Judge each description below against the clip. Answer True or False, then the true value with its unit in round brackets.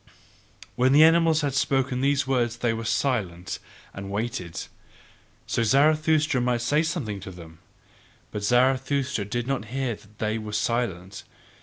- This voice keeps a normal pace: True (155 wpm)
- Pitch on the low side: True (120 Hz)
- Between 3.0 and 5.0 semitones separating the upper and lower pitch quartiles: True (4.6 semitones)